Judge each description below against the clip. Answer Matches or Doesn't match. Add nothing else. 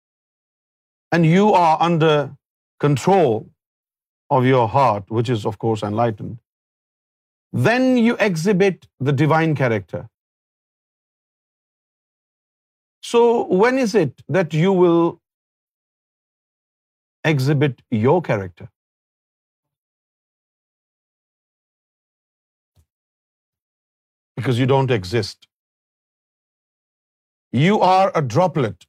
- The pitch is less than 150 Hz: Matches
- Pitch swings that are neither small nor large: Doesn't match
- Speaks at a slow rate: Matches